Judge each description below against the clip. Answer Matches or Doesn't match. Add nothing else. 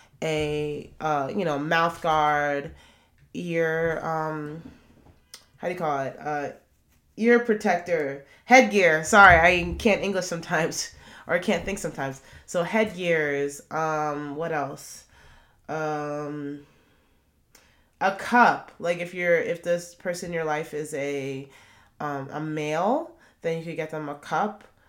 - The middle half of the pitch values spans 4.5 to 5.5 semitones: Doesn't match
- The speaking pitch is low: Doesn't match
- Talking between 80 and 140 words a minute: Matches